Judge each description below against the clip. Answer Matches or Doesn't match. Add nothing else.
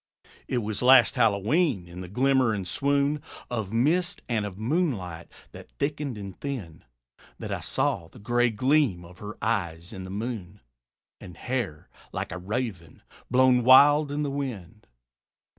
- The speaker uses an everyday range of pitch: Doesn't match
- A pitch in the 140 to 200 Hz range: Doesn't match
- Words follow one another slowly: Doesn't match